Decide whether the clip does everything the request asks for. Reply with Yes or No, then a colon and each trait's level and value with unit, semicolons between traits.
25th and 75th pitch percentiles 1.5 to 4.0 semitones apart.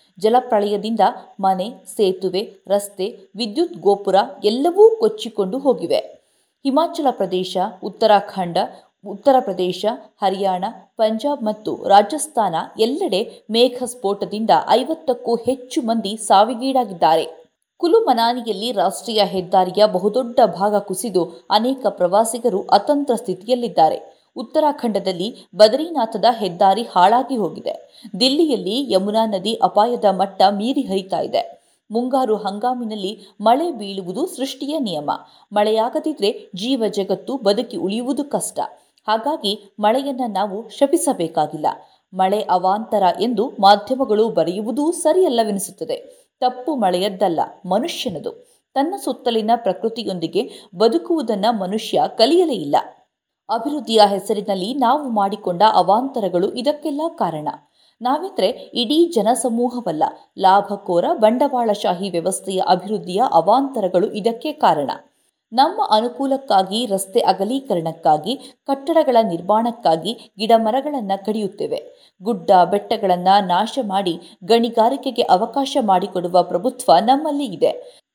No: average, 5.1 semitones